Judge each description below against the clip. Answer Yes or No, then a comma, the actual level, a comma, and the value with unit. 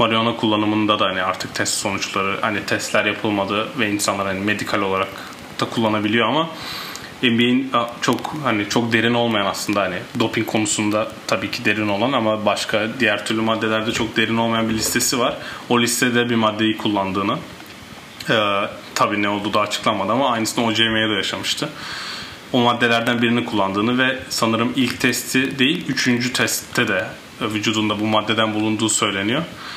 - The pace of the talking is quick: Yes, fast, 155 wpm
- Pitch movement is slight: Yes, narrow, 1.9 semitones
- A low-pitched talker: Yes, low, 110 Hz